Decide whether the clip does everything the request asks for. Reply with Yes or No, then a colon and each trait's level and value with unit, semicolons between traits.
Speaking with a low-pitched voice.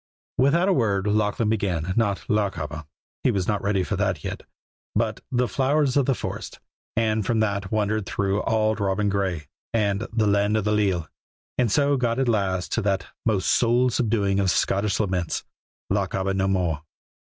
Yes: low, 105 Hz